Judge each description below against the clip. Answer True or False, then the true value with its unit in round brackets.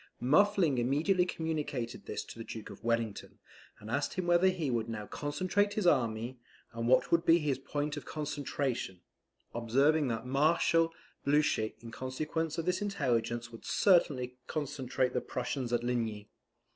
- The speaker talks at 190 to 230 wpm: False (155 wpm)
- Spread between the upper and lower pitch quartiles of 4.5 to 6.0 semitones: True (5.5 semitones)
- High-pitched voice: False (135 Hz)